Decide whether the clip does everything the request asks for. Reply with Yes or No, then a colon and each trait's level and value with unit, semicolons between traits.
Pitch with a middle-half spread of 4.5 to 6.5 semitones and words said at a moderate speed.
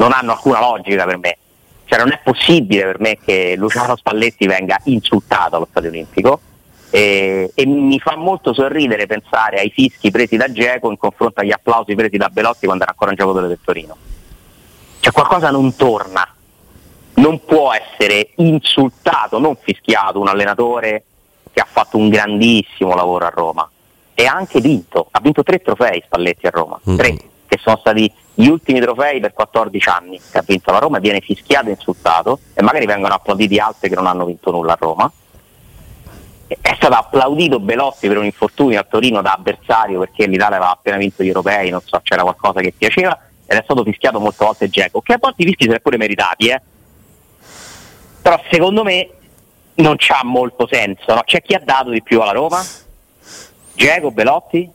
No: average, 5.3 semitones; fast, 180 wpm